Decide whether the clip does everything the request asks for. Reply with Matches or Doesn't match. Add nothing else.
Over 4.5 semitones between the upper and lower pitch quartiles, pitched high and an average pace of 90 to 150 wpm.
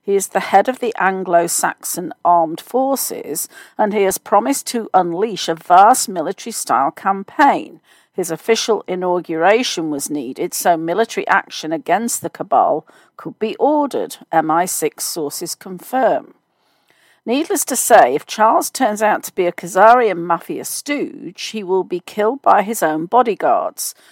Matches